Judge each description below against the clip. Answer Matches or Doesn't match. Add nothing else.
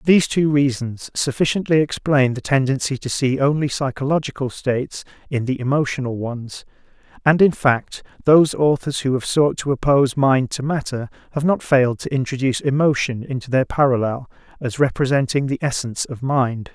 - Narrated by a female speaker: Doesn't match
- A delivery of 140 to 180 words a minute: Matches